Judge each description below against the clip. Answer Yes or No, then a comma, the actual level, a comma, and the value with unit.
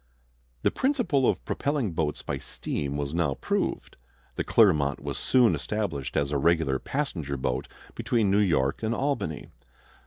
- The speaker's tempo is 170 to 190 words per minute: No, average, 150 wpm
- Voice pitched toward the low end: Yes, very low, 85 Hz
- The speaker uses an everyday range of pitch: No, wide, 8.7 semitones